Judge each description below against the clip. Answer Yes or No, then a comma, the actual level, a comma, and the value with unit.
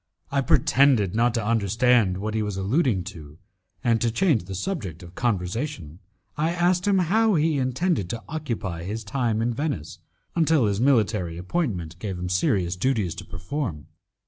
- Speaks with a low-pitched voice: Yes, low, 115 Hz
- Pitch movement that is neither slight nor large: No, wide, 7.4 semitones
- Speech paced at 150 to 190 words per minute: Yes, average, 165 wpm